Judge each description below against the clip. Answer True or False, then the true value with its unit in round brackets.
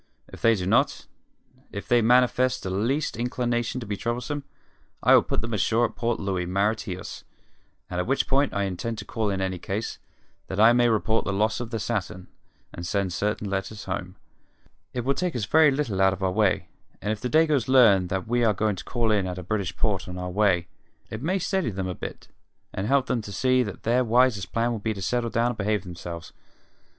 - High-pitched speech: False (110 Hz)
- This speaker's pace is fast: True (220 wpm)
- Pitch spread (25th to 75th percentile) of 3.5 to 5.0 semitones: True (4.0 semitones)